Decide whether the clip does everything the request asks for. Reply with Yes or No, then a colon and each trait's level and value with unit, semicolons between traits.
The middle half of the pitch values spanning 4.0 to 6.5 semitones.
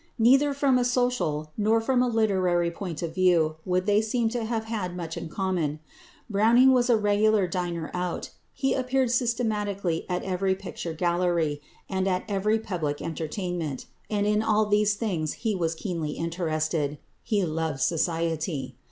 Yes: average, 4.8 semitones